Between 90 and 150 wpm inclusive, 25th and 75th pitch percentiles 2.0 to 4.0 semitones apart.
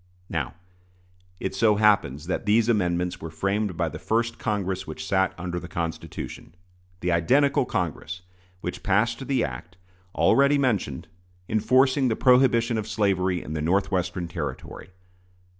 No: average, 140 wpm; average, 5.0 semitones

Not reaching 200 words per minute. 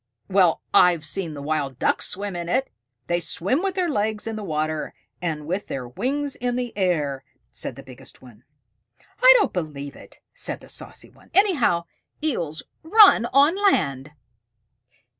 Yes: average, 160 wpm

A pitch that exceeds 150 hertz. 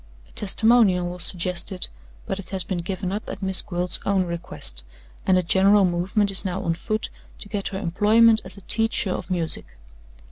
Yes: high, 190 Hz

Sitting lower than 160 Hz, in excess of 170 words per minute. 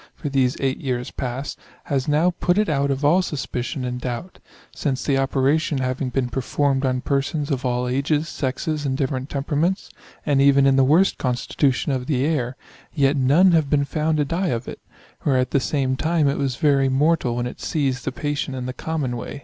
Yes: medium, 140 Hz; average, 200 wpm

